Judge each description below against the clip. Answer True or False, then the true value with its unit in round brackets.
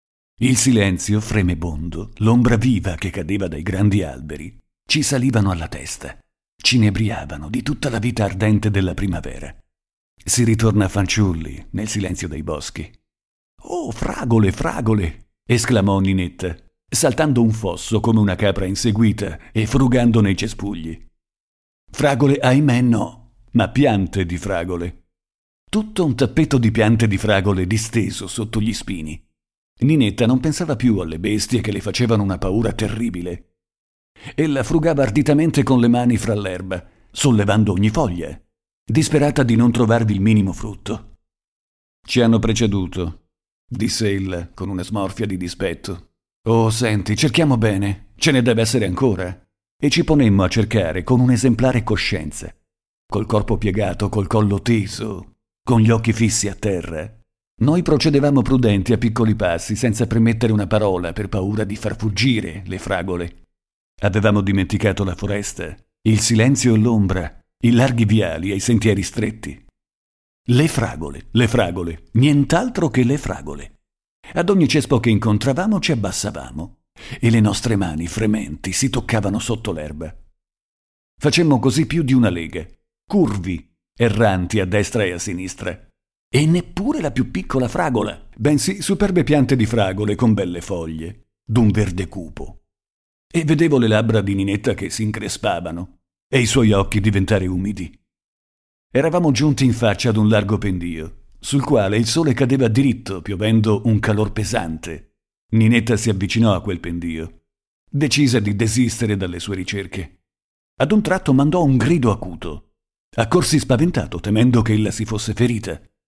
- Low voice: True (110 Hz)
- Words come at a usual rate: True (145 wpm)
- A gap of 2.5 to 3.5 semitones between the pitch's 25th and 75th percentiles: False (4.3 semitones)